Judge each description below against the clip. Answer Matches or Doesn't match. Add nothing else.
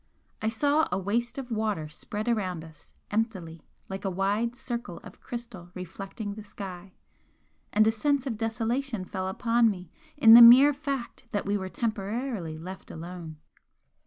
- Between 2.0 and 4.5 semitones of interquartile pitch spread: Matches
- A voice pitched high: Matches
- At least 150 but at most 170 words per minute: Matches